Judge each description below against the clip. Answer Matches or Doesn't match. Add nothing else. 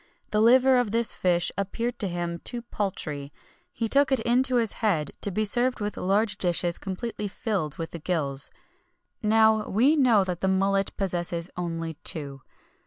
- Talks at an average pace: Matches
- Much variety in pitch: Doesn't match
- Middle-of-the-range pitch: Doesn't match